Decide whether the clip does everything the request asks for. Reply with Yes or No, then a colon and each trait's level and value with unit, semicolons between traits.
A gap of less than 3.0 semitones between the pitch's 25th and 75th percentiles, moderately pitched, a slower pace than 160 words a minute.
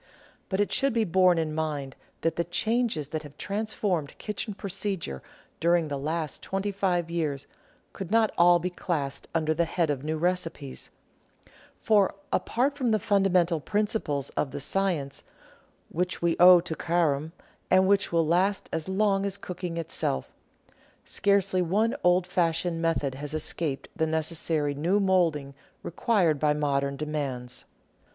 No: average, 4.1 semitones; medium, 170 Hz; average, 150 wpm